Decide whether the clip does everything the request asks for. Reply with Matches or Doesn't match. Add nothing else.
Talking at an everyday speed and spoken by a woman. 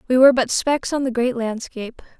Doesn't match